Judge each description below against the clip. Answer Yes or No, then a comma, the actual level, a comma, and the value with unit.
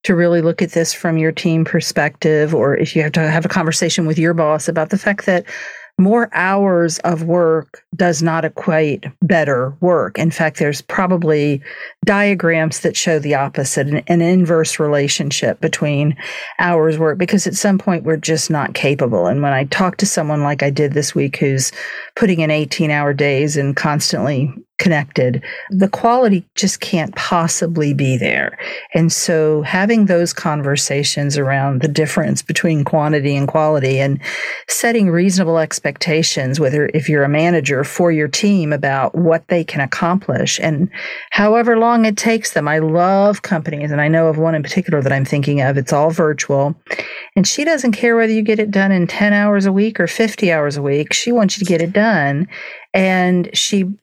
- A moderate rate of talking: Yes, average, 180 wpm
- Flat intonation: No, average, 4.0 semitones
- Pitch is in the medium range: Yes, medium, 165 Hz